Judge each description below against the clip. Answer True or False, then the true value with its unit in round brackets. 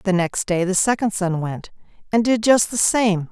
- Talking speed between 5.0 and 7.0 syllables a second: False (4.7 syllables/s)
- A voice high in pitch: True (200 Hz)